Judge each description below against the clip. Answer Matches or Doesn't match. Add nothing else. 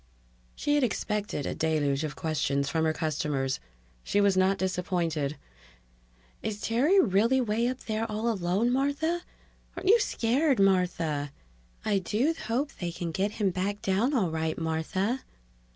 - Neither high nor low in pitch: Doesn't match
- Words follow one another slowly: Doesn't match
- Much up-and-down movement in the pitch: Matches